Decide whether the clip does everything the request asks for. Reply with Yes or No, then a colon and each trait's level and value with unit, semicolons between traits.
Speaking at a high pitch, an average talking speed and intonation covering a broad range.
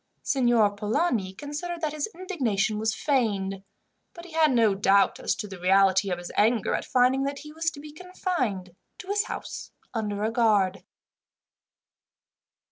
Yes: high, 230 Hz; average, 160 wpm; wide, 7.2 semitones